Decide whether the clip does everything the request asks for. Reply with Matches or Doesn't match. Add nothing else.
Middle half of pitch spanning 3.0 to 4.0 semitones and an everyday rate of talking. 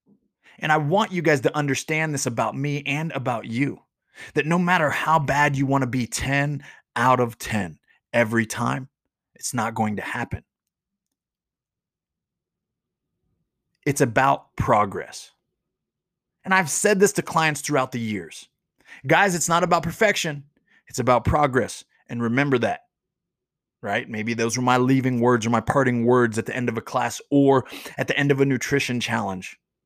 Doesn't match